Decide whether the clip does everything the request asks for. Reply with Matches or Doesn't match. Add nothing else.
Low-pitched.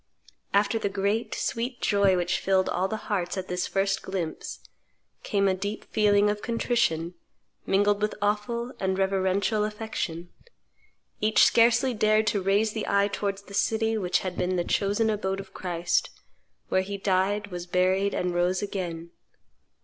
Doesn't match